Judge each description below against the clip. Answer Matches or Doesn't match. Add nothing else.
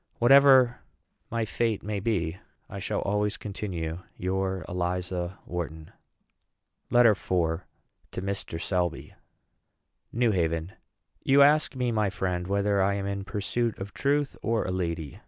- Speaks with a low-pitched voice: Matches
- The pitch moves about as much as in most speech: Matches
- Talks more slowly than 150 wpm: Matches